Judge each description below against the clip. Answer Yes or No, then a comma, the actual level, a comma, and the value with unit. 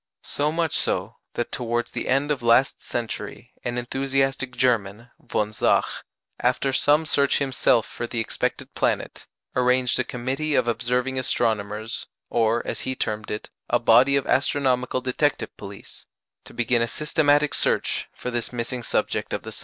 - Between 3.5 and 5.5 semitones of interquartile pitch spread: No, narrow, 2.6 semitones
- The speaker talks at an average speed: Yes, average, 160 wpm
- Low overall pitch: Yes, low, 125 Hz